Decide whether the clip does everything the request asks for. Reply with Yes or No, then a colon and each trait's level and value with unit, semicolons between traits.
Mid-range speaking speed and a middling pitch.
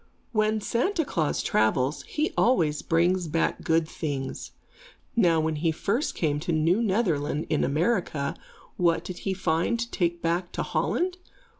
Yes: average, 150 wpm; medium, 170 Hz